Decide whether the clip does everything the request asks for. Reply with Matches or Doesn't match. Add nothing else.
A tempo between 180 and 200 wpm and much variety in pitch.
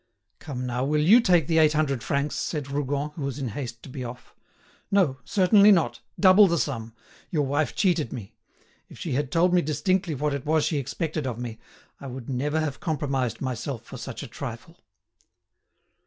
Doesn't match